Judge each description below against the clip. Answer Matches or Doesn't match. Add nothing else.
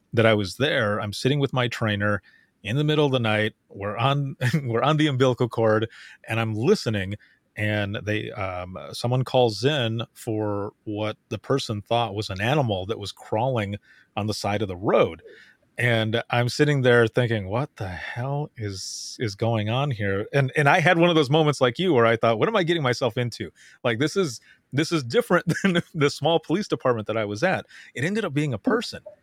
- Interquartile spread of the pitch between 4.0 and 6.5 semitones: Matches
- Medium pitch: Doesn't match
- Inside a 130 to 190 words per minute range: Doesn't match